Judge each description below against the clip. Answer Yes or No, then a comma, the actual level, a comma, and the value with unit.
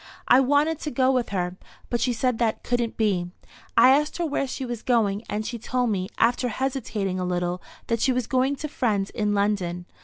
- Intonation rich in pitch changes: No, average, 4.5 semitones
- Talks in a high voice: Yes, high, 235 Hz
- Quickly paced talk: Yes, fast, 210 wpm